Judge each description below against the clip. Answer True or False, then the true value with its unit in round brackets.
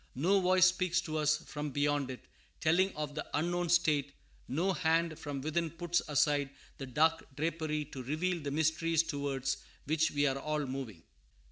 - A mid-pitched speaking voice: True (155 Hz)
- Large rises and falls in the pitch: False (2.8 semitones)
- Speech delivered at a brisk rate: False (165 wpm)